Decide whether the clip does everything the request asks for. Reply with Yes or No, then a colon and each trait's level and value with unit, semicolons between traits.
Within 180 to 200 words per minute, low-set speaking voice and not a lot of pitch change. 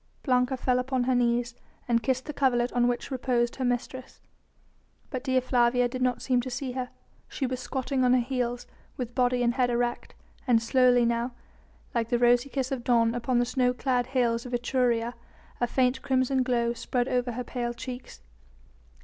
No: average, 185 wpm; high, 245 Hz; narrow, 1.2 semitones